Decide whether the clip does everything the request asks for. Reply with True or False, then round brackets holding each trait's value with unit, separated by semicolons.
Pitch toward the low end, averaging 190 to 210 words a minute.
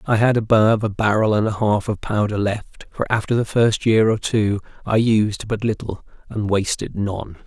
True (105 Hz; 200 wpm)